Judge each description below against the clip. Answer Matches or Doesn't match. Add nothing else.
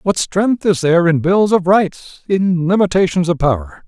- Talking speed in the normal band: Matches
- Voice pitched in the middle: Matches